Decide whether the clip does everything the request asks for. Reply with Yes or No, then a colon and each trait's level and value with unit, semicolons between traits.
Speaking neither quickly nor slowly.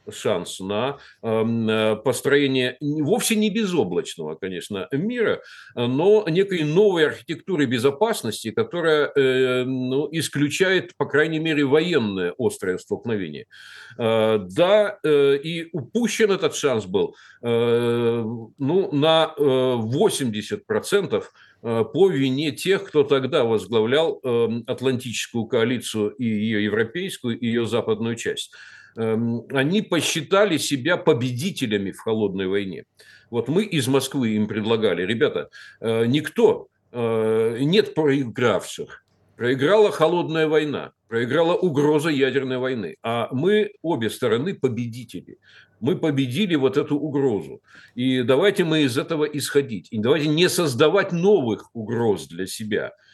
No: slow, 105 wpm